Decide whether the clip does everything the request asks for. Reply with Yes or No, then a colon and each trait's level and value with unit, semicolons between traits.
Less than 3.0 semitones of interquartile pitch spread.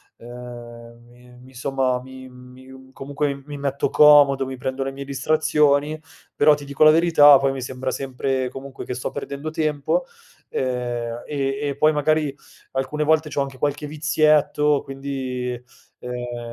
Yes: narrow, 2.6 semitones